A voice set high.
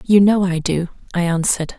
No: medium, 180 Hz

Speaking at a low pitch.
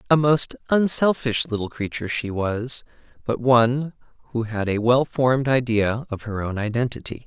Yes: low, 120 Hz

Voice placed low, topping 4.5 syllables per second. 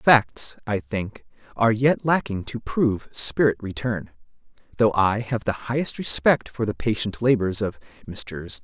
No: low, 110 Hz; 4.3 syllables/s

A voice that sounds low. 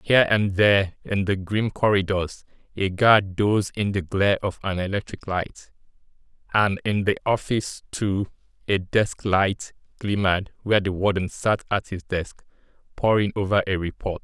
Yes: low, 100 Hz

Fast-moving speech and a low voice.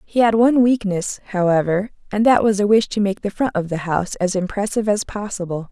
No: fast, 220 wpm; high, 200 Hz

